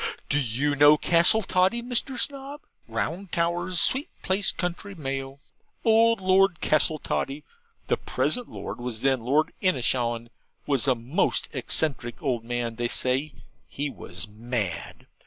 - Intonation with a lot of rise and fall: Yes, wide, 7.3 semitones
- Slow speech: Yes, slow, 130 wpm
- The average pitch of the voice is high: No, medium, 145 Hz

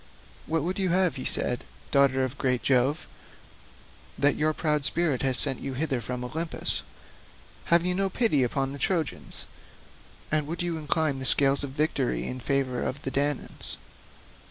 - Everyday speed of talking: Yes, average, 165 wpm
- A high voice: No, medium, 145 Hz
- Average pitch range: Yes, average, 3.4 semitones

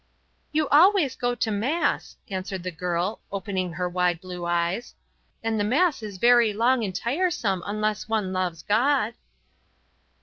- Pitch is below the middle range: No, high, 210 Hz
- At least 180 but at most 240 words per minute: No, average, 145 wpm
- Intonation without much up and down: No, average, 4.9 semitones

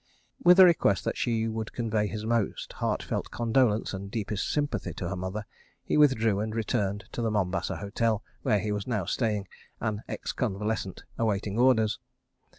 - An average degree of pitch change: No, narrow, 2.3 semitones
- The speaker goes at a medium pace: Yes, average, 170 wpm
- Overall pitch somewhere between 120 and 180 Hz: No, low, 110 Hz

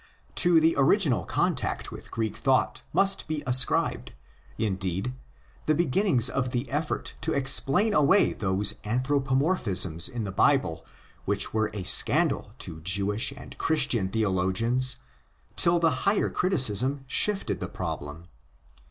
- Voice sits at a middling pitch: No, low, 130 Hz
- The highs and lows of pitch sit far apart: Yes, wide, 7.0 semitones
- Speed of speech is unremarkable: No, slow, 125 wpm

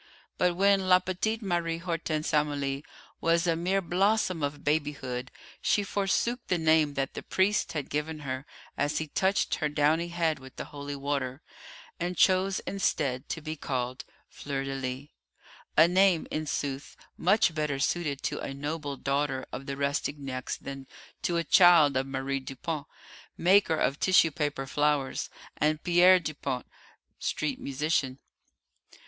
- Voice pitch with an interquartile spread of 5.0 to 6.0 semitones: No, average, 3.9 semitones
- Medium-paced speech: Yes, average, 150 wpm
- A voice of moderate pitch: Yes, medium, 150 Hz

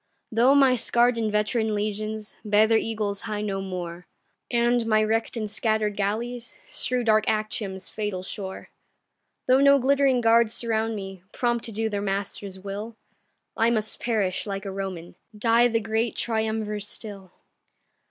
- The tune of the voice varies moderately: No, narrow, 2.3 semitones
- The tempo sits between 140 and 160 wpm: Yes, average, 150 wpm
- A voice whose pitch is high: Yes, high, 215 Hz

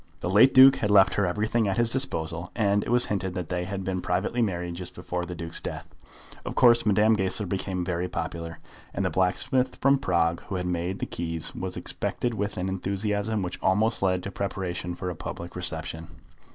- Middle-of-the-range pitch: No, very low, 95 Hz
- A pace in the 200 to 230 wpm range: Yes, fast, 205 wpm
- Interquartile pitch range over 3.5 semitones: No, average, 3.0 semitones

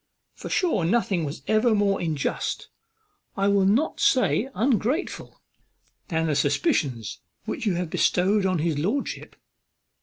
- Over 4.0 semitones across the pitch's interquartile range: Yes, average, 5.2 semitones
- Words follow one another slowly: Yes, slow, 130 wpm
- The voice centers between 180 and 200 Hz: Yes, high, 190 Hz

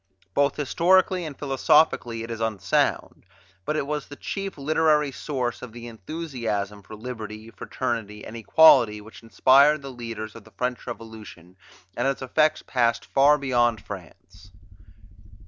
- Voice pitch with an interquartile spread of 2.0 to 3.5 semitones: No, average, 4.6 semitones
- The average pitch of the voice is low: Yes, low, 120 Hz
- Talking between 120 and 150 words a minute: Yes, average, 145 wpm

